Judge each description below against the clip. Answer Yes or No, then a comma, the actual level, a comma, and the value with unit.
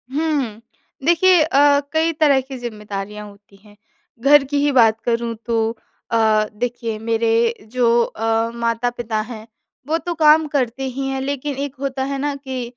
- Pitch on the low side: No, high, 245 Hz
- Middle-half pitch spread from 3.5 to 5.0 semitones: Yes, average, 3.8 semitones